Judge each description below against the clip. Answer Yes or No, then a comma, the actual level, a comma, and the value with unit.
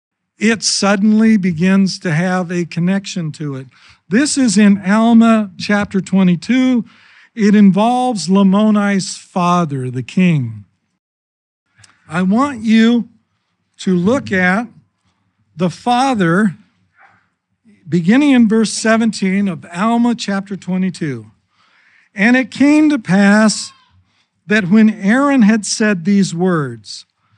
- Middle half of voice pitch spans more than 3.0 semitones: Yes, average, 4.1 semitones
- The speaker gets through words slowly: Yes, slow, 105 wpm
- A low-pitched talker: No, high, 195 Hz